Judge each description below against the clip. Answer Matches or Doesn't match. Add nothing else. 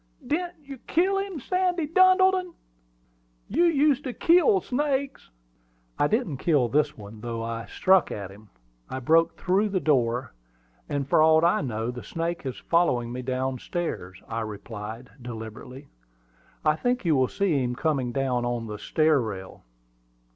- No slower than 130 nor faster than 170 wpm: Matches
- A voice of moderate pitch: Matches